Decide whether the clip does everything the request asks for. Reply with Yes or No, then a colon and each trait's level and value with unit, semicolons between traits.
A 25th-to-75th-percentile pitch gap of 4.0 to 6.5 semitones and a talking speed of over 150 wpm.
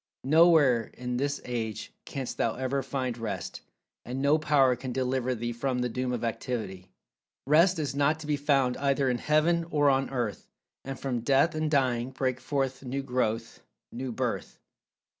No: narrow, 2.5 semitones; average, 165 wpm